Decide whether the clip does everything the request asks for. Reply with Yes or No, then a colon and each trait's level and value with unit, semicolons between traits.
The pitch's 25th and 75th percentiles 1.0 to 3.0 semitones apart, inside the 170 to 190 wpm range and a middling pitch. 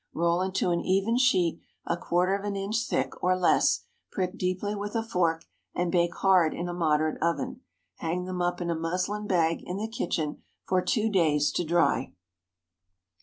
Yes: narrow, 2.6 semitones; average, 180 wpm; medium, 180 Hz